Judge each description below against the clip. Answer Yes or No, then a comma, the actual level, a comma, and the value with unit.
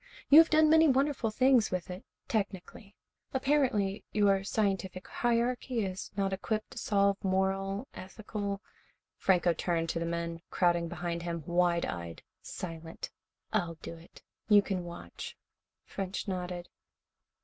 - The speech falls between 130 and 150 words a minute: Yes, average, 140 wpm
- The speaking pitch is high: Yes, high, 195 Hz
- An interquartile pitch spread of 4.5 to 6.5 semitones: No, average, 3.8 semitones